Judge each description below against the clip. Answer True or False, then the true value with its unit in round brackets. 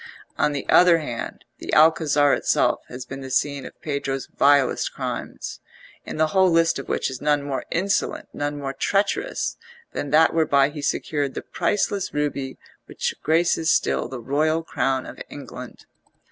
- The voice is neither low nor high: True (145 Hz)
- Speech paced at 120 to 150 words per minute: False (160 wpm)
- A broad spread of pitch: False (2.9 semitones)